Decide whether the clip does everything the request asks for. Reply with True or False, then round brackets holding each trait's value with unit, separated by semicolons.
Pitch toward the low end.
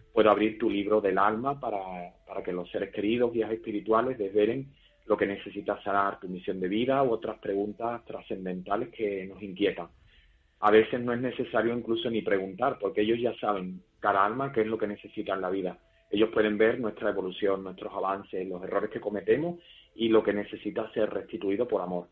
True (105 Hz)